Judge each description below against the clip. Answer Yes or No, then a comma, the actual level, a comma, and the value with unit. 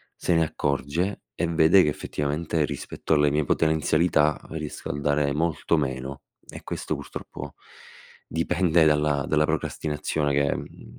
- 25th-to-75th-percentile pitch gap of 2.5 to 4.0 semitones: No, narrow, 2.1 semitones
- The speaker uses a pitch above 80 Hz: No, very low, 75 Hz